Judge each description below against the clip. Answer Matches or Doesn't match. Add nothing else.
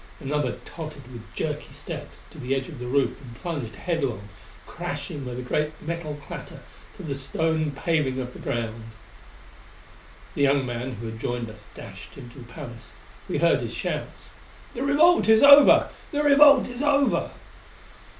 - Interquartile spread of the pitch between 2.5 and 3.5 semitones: Doesn't match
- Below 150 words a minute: Doesn't match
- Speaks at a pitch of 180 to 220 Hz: Doesn't match